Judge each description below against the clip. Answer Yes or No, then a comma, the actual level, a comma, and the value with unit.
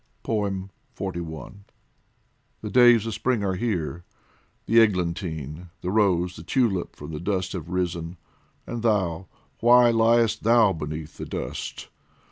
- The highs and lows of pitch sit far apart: No, average, 4.8 semitones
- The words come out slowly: Yes, slow, 125 wpm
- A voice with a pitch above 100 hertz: No, very low, 95 Hz